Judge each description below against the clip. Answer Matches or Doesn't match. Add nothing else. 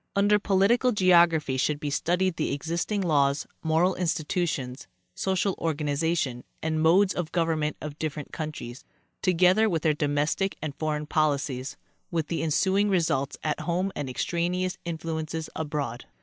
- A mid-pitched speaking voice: Matches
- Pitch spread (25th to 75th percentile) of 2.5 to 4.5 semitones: Matches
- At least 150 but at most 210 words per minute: Doesn't match